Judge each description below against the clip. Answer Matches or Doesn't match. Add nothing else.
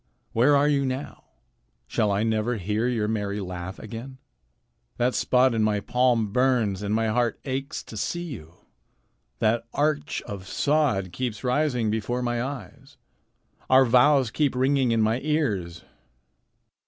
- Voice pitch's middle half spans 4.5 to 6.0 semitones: Doesn't match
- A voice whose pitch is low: Matches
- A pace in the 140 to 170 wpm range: Matches